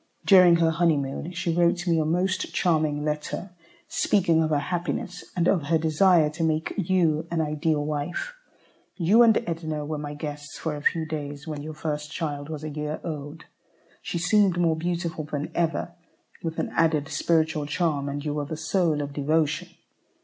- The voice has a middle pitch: Yes, medium, 160 Hz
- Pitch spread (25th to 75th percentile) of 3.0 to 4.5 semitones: No, narrow, 2.4 semitones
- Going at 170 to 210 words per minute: Yes, average, 180 wpm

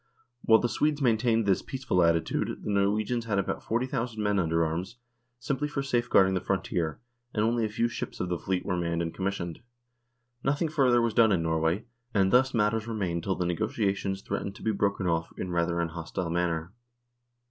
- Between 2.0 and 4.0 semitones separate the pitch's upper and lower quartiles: No, average, 5.0 semitones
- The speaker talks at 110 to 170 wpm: No, average, 190 wpm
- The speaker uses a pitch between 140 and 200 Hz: No, low, 100 Hz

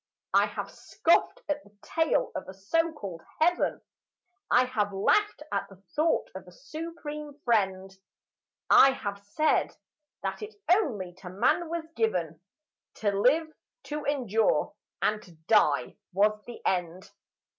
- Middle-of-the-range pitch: No, high, 225 Hz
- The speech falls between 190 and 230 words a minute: No, average, 140 wpm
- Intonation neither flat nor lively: No, wide, 8.0 semitones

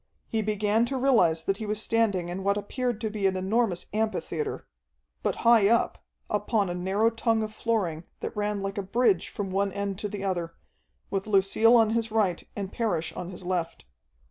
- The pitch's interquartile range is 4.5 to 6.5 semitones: No, average, 2.9 semitones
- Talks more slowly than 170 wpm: No, average, 195 wpm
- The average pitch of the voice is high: Yes, high, 205 Hz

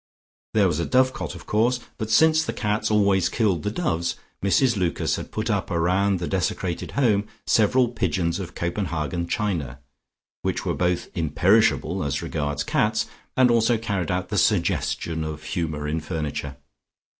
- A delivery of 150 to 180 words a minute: Yes, average, 155 wpm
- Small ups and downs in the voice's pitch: No, average, 4.8 semitones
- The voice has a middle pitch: No, very low, 95 Hz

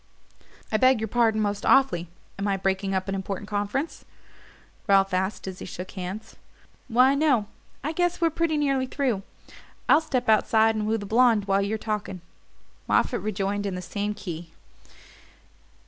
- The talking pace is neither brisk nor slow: Yes, average, 160 wpm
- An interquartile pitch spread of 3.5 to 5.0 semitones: Yes, average, 4.6 semitones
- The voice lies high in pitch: Yes, high, 210 Hz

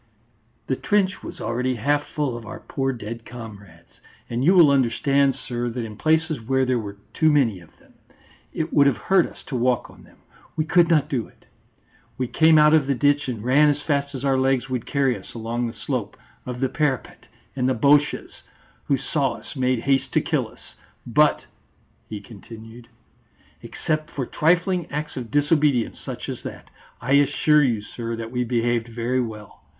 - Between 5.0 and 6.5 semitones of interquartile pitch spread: No, average, 3.8 semitones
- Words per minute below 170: No, average, 190 wpm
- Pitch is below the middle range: Yes, low, 130 Hz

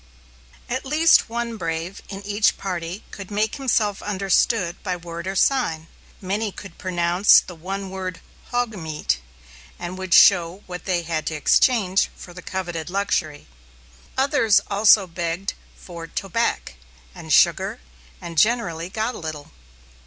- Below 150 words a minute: Yes, average, 140 wpm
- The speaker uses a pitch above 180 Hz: Yes, high, 190 Hz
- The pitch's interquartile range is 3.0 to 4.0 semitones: Yes, average, 3.6 semitones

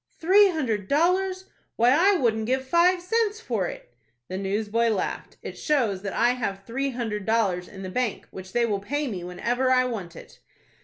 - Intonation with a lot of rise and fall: Yes, wide, 6.8 semitones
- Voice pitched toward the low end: No, high, 240 Hz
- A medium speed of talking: Yes, average, 190 wpm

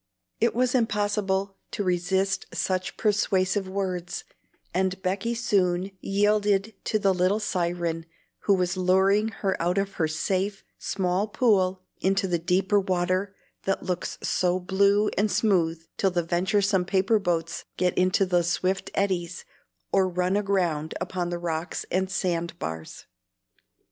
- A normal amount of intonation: No, narrow, 2.0 semitones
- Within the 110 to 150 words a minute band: Yes, slow, 135 wpm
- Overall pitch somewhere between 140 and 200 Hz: Yes, high, 190 Hz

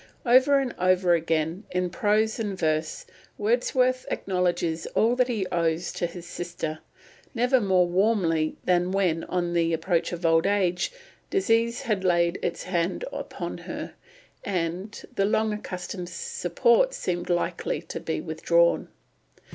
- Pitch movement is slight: No, average, 4.4 semitones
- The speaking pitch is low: No, medium, 185 Hz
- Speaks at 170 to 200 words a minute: No, average, 140 wpm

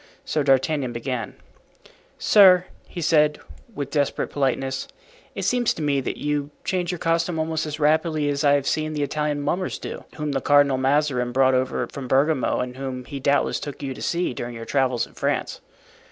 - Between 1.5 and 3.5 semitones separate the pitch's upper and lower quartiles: Yes, average, 2.8 semitones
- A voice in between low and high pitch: Yes, medium, 145 Hz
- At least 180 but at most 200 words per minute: Yes, average, 185 wpm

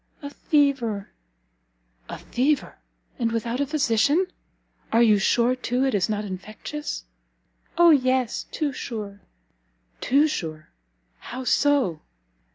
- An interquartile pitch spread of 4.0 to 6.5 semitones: Yes, average, 5.0 semitones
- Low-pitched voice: No, very high, 250 Hz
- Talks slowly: Yes, slow, 115 wpm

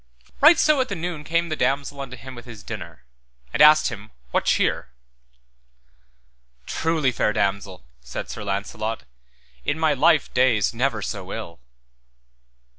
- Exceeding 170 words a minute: No, average, 145 wpm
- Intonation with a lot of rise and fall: Yes, wide, 6.9 semitones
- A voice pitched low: Yes, low, 125 Hz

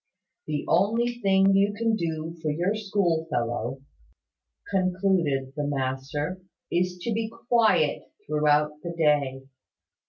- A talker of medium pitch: Yes, medium, 170 Hz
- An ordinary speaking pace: No, slow, 125 wpm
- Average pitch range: Yes, average, 5.0 semitones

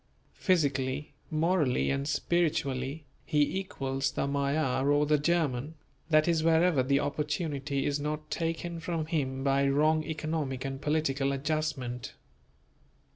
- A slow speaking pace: Yes, slow, 125 wpm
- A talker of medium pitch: Yes, medium, 150 Hz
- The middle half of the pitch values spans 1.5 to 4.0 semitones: Yes, narrow, 2.6 semitones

